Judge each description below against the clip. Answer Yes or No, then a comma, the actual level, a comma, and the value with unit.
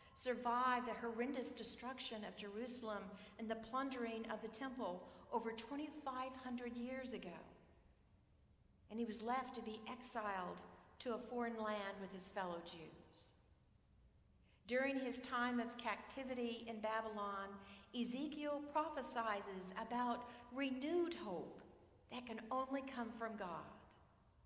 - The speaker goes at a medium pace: No, slow, 120 wpm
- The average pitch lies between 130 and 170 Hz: No, high, 235 Hz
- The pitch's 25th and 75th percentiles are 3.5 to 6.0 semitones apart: No, average, 2.9 semitones